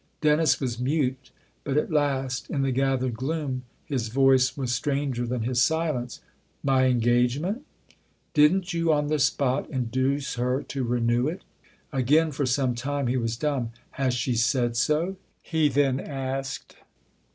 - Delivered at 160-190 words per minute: Yes, average, 165 wpm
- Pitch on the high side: No, low, 135 Hz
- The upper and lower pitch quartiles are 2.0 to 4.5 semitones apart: Yes, average, 2.9 semitones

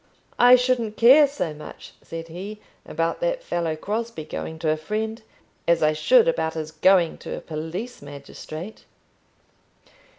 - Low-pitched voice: No, medium, 175 Hz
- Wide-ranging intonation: Yes, wide, 6.8 semitones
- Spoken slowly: No, average, 145 wpm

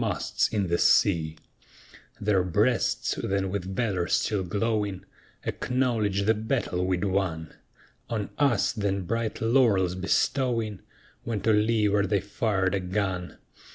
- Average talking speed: No, slow, 110 wpm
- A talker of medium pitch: No, low, 100 Hz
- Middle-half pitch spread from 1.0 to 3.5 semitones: Yes, average, 3.0 semitones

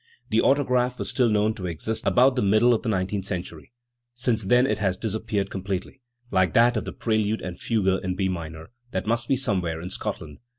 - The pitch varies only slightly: No, average, 4.2 semitones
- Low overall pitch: Yes, low, 105 Hz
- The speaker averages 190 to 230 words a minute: Yes, fast, 205 wpm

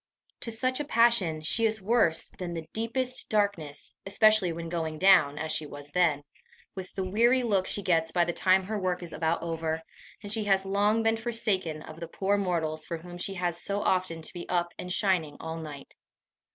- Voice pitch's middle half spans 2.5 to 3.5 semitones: No, average, 4.2 semitones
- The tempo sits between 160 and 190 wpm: No, fast, 205 wpm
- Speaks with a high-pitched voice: No, medium, 180 Hz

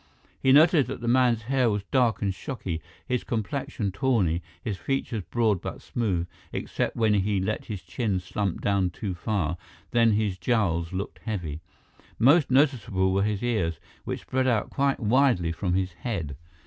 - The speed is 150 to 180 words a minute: Yes, average, 165 wpm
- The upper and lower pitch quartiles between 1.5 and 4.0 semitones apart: No, average, 4.8 semitones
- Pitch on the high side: No, low, 105 Hz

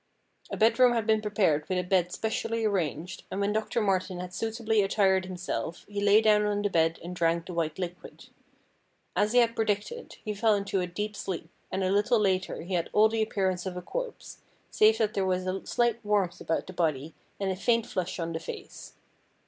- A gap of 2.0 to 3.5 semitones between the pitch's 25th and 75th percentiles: Yes, average, 3.2 semitones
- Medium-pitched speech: No, high, 195 Hz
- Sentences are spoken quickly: Yes, fast, 210 wpm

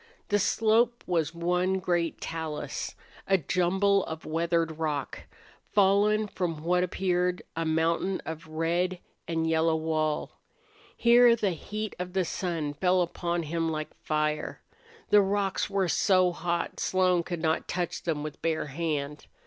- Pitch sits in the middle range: Yes, medium, 175 Hz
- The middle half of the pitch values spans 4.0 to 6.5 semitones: No, average, 2.8 semitones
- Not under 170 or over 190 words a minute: No, average, 140 wpm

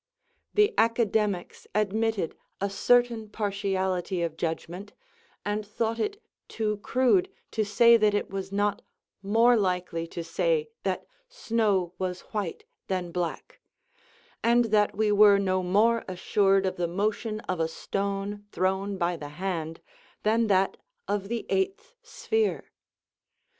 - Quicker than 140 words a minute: No, slow, 135 wpm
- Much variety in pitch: No, average, 3.3 semitones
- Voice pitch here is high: Yes, high, 205 Hz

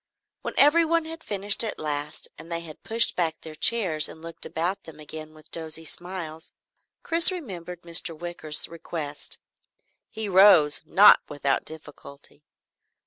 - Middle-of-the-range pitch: Yes, medium, 170 Hz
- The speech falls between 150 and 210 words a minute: No, average, 140 wpm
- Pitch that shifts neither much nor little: Yes, average, 4.5 semitones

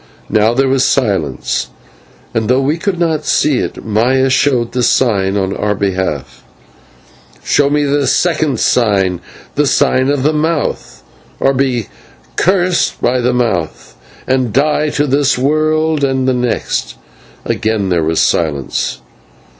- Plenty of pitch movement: Yes, wide, 5.7 semitones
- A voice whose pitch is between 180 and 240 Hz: No, low, 130 Hz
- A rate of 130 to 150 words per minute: Yes, average, 140 wpm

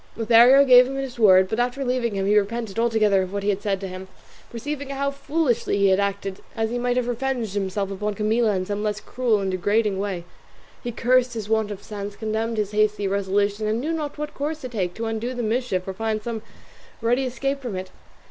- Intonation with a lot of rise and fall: No, average, 3.5 semitones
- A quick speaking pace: Yes, fast, 225 wpm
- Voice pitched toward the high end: Yes, high, 220 Hz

